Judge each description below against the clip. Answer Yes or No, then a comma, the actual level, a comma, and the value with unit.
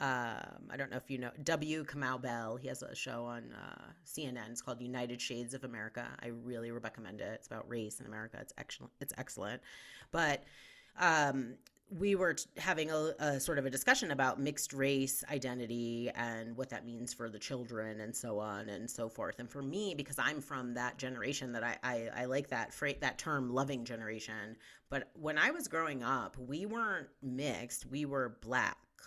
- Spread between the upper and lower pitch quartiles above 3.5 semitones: No, average, 2.9 semitones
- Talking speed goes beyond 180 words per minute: Yes, average, 200 wpm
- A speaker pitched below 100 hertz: No, low, 125 Hz